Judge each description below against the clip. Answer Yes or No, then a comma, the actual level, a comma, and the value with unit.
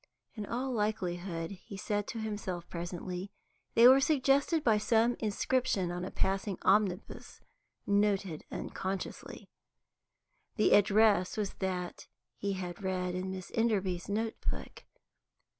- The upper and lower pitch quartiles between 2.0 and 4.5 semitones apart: Yes, average, 3.1 semitones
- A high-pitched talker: Yes, high, 200 Hz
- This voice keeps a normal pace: No, slow, 125 wpm